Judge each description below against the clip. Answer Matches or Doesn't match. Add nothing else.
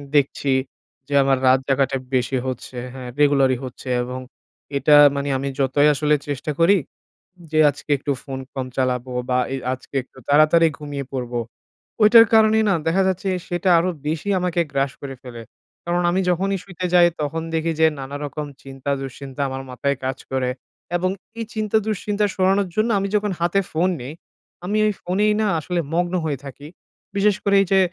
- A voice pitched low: Doesn't match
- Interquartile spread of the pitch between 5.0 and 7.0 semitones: Matches